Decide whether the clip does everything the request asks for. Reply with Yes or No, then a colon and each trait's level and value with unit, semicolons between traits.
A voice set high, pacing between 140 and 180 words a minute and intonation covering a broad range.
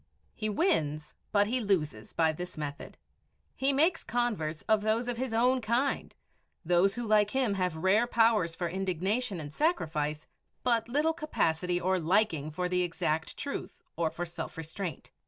Yes: high, 195 Hz; average, 160 wpm; wide, 6.6 semitones